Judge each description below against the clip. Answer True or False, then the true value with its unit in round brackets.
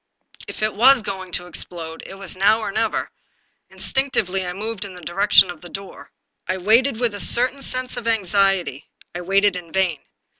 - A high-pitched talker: True (195 Hz)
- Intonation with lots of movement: False (3.7 semitones)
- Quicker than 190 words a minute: False (185 wpm)